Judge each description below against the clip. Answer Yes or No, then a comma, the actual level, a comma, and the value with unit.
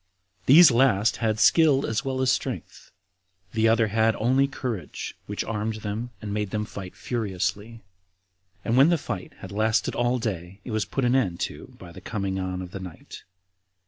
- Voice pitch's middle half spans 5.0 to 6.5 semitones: No, average, 3.8 semitones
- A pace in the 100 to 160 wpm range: No, average, 180 wpm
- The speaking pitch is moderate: No, low, 110 Hz